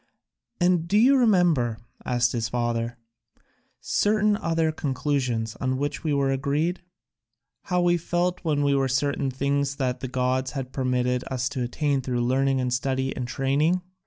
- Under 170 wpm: Yes, average, 155 wpm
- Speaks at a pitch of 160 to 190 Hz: No, low, 135 Hz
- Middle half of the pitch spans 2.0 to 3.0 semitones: No, average, 4.1 semitones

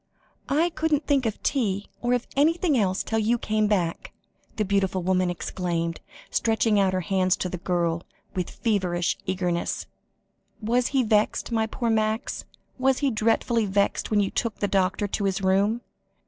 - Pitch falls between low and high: No, high, 210 Hz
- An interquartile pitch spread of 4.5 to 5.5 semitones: No, average, 3.9 semitones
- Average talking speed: Yes, average, 165 wpm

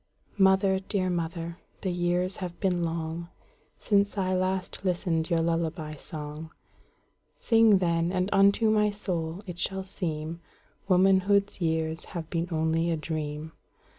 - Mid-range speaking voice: Yes, medium, 175 Hz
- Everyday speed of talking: No, slow, 120 wpm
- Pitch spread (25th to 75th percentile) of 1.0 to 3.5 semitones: Yes, average, 2.8 semitones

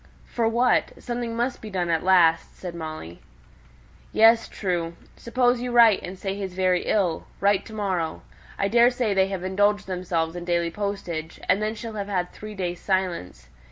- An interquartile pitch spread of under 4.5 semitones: Yes, average, 3.8 semitones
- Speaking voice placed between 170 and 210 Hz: Yes, high, 190 Hz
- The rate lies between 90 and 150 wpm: No, average, 170 wpm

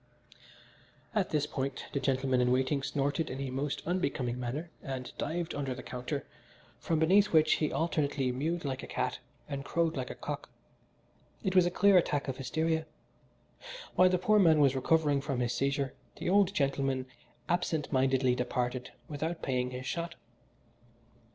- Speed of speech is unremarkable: Yes, average, 165 wpm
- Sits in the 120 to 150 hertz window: Yes, medium, 140 Hz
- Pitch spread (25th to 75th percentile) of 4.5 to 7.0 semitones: No, average, 3.9 semitones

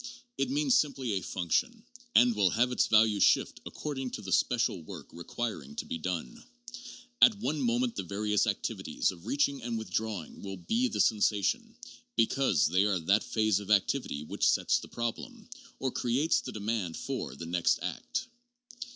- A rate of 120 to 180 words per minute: Yes, average, 170 wpm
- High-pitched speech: No, low, 110 Hz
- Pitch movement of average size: No, wide, 6.0 semitones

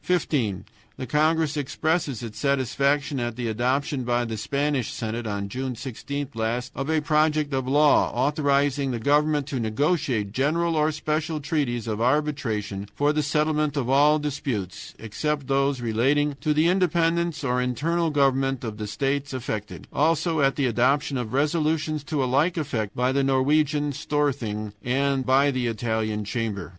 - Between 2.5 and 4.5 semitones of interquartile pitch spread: Yes, average, 3.8 semitones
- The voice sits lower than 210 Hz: Yes, medium, 140 Hz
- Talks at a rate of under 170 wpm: Yes, average, 160 wpm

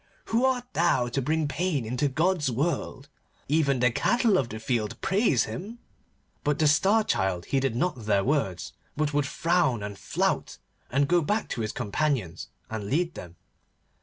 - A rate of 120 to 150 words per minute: No, average, 165 wpm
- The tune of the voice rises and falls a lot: Yes, wide, 7.0 semitones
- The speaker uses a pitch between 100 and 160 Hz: Yes, medium, 140 Hz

